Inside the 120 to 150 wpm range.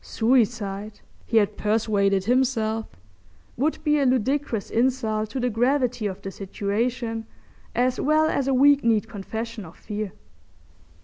Yes: slow, 135 wpm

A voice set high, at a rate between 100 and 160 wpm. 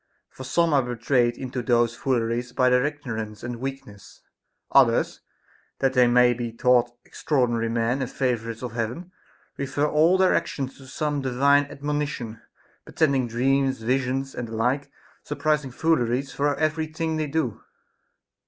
No: low, 130 Hz; average, 145 wpm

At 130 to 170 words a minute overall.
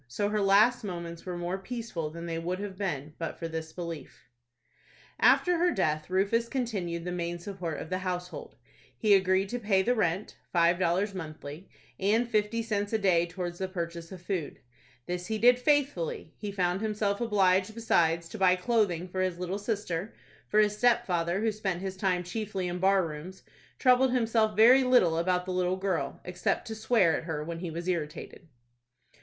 No: average, 180 wpm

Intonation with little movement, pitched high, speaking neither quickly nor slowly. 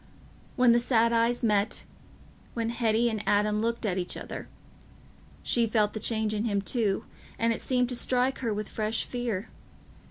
Yes: narrow, 2.0 semitones; high, 230 Hz; average, 160 wpm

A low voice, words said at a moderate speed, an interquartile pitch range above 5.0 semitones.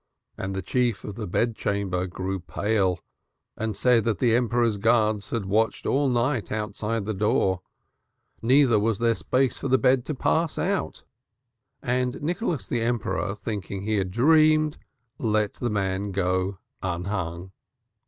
No: low, 110 Hz; average, 150 wpm; average, 4.0 semitones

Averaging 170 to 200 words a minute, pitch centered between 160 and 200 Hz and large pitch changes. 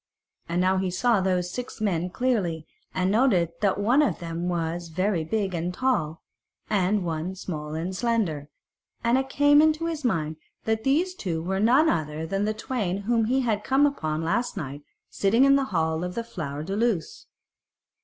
Yes: average, 185 wpm; high, 190 Hz; wide, 6.2 semitones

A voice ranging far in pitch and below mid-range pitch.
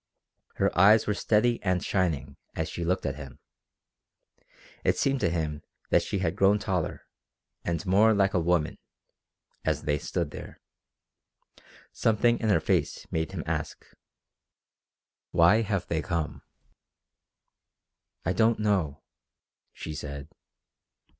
No: average, 4.6 semitones; very low, 90 Hz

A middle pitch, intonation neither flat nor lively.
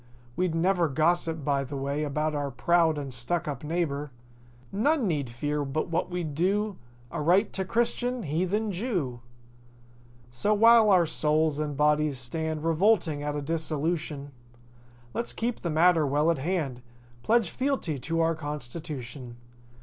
Yes: medium, 160 Hz; average, 3.8 semitones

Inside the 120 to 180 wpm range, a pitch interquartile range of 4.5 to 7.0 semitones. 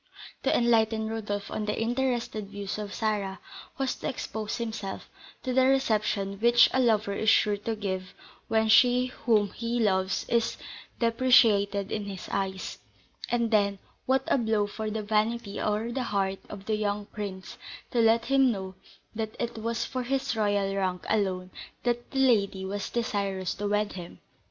No: average, 165 wpm; average, 2.7 semitones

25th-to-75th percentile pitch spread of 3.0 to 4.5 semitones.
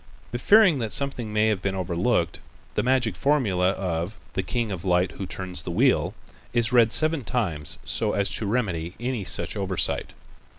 No: average, 5.1 semitones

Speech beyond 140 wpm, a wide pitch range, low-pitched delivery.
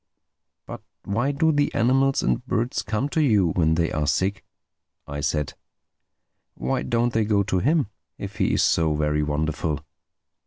Yes: average, 155 wpm; wide, 8.5 semitones; low, 100 Hz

